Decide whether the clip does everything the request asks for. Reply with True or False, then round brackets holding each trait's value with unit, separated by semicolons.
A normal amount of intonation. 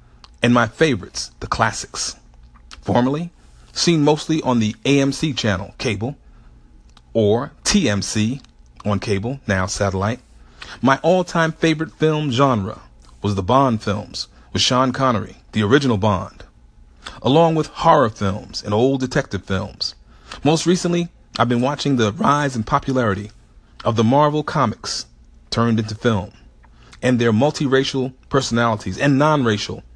False (6.1 semitones)